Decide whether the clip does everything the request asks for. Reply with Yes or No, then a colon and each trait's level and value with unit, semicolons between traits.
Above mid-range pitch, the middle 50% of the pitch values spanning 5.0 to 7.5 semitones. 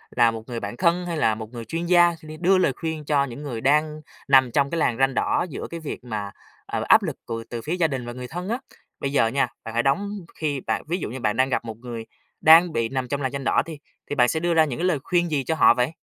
No: medium, 140 Hz; average, 5.3 semitones